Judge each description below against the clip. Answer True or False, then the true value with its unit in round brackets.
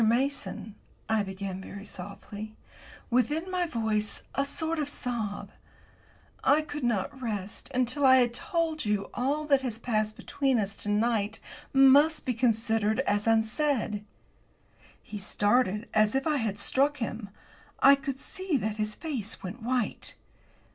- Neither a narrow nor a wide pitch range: True (4.7 semitones)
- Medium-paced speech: True (150 wpm)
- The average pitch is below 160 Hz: False (235 Hz)